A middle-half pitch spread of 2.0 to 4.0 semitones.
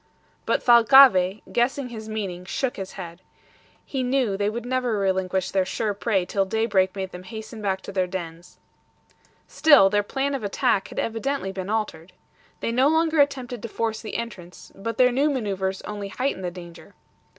No: average, 4.5 semitones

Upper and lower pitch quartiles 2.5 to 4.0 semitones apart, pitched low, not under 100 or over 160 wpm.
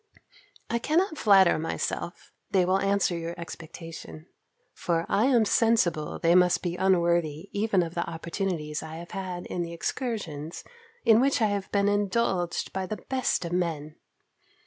No: average, 3.4 semitones; medium, 180 Hz; average, 155 wpm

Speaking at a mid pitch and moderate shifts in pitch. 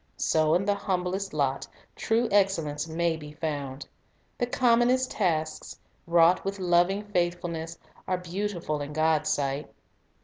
Yes: medium, 175 Hz; average, 4.0 semitones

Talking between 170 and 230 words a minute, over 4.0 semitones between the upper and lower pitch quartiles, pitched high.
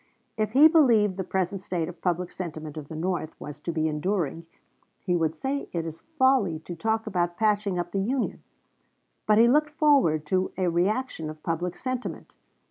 No: average, 185 wpm; average, 5.1 semitones; medium, 180 Hz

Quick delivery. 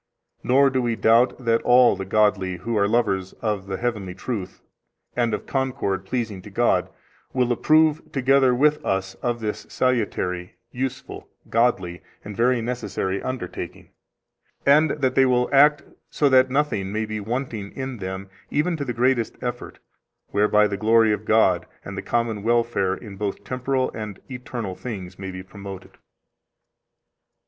No: average, 155 wpm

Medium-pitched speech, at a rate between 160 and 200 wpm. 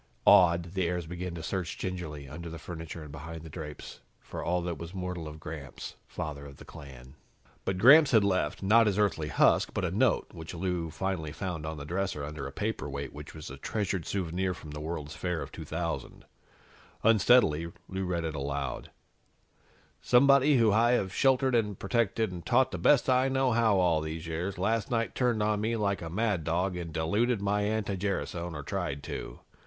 No: very low, 90 Hz; average, 195 wpm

